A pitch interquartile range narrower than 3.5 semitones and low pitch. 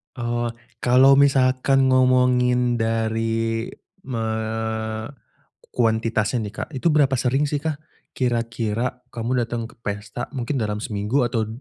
Yes: narrow, 2.4 semitones; low, 120 Hz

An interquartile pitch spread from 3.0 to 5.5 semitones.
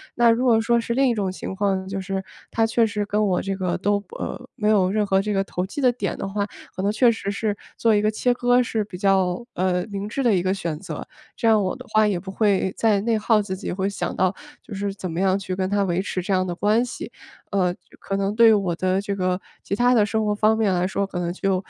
No: narrow, 2.6 semitones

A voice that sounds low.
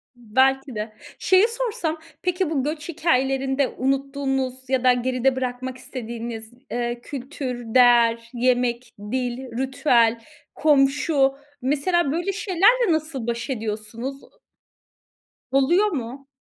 No: very high, 265 Hz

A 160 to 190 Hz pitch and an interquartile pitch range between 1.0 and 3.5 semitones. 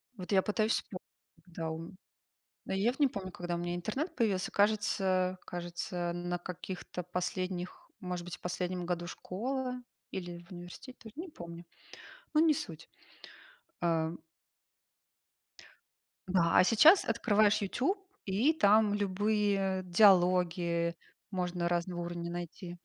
Yes: medium, 185 Hz; average, 3.2 semitones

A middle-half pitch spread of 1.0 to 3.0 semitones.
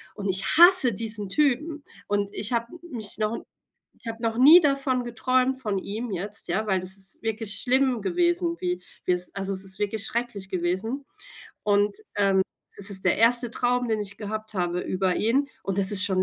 No: average, 4.2 semitones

